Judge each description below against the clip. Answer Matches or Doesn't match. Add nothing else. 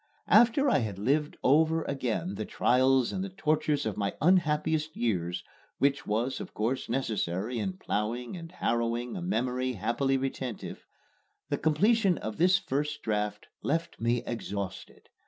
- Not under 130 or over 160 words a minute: Matches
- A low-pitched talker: Matches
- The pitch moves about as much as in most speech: Doesn't match